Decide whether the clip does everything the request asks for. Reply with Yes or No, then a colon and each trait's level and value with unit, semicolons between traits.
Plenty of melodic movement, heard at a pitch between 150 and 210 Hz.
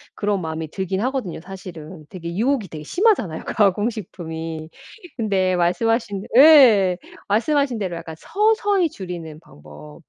Yes: wide, 6.2 semitones; high, 190 Hz